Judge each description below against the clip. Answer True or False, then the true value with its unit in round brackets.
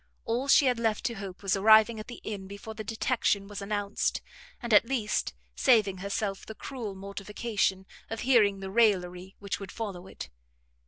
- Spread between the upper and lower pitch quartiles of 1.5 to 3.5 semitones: True (2.5 semitones)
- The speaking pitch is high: True (210 Hz)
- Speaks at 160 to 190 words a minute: True (175 wpm)